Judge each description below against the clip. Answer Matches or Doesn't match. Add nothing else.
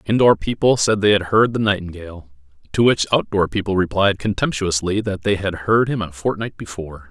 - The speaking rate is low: Doesn't match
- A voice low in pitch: Matches